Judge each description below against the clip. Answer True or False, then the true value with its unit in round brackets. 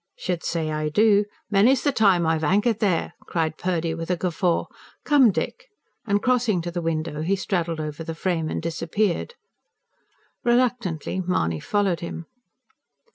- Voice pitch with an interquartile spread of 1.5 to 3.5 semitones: False (4.2 semitones)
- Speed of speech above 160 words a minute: False (150 wpm)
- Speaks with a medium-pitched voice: True (180 Hz)